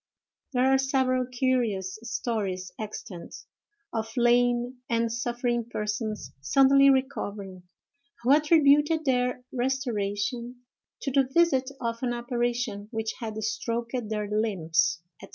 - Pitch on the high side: Yes, high, 240 Hz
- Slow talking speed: Yes, slow, 115 wpm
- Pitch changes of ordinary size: Yes, average, 3.3 semitones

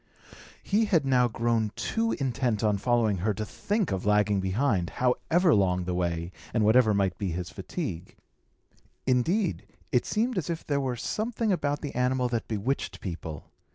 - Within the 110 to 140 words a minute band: No, average, 165 wpm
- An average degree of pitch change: No, wide, 6.5 semitones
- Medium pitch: No, low, 120 Hz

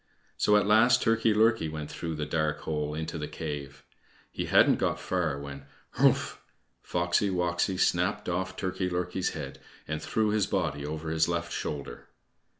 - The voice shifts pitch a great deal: No, average, 3.6 semitones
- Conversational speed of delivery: Yes, average, 160 wpm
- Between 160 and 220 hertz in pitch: No, very low, 85 Hz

